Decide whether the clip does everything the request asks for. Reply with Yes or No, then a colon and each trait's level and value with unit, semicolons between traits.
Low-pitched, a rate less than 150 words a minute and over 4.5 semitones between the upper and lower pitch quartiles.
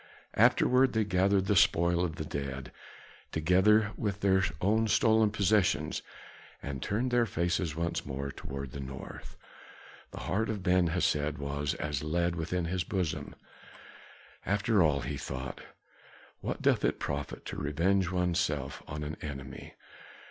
Yes: very low, 85 Hz; average, 140 wpm; average, 5.3 semitones